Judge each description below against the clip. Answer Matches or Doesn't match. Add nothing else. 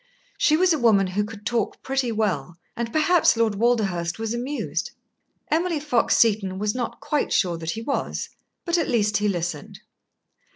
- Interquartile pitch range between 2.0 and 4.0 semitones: Doesn't match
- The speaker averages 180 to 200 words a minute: Doesn't match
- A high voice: Matches